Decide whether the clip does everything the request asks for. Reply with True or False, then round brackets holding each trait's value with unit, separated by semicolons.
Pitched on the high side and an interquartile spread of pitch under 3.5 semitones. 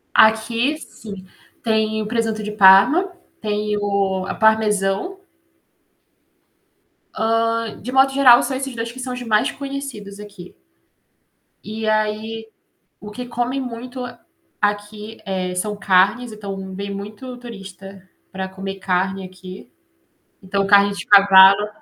True (210 Hz; 3.1 semitones)